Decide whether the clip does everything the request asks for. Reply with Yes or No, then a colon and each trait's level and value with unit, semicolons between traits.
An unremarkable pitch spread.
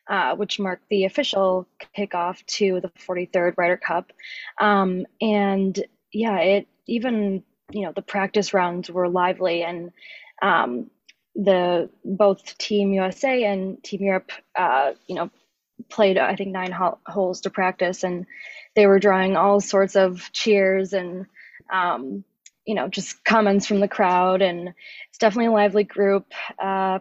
No: narrow, 2.0 semitones